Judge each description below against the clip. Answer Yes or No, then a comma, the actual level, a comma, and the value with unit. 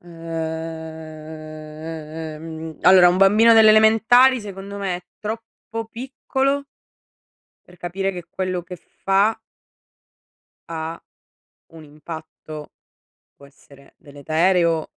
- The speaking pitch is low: No, medium, 170 Hz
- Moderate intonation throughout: Yes, average, 4.2 semitones